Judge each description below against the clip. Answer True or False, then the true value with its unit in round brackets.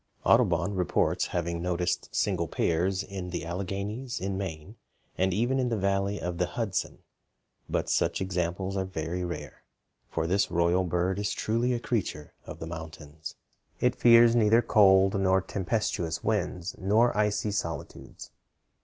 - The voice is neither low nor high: False (95 Hz)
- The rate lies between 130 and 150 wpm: True (145 wpm)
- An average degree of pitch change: True (3.2 semitones)